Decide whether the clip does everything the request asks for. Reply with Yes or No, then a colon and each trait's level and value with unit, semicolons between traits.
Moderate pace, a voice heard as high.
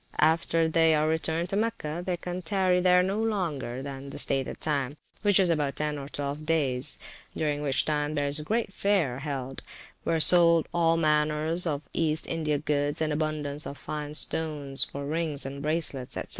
No: average, 185 wpm; medium, 155 Hz